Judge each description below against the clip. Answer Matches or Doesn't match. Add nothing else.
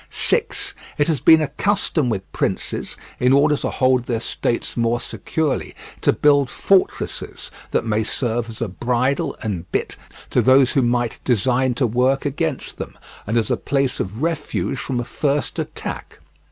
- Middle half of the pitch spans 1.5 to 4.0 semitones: Matches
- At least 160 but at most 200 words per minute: Matches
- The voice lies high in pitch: Doesn't match